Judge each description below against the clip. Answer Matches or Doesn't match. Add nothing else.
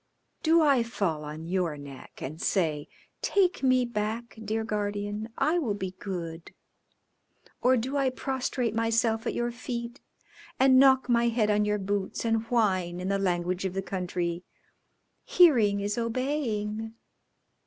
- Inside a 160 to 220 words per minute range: Doesn't match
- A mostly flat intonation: Doesn't match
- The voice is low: Doesn't match